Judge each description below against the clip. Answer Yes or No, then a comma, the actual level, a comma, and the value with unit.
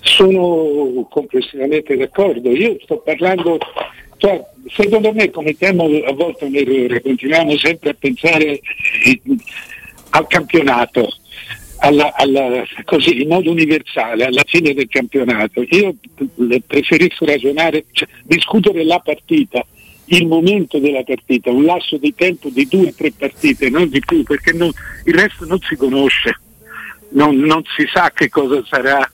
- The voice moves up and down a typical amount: Yes, average, 4.5 semitones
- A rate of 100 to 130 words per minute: No, average, 140 wpm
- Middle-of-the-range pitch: Yes, medium, 155 Hz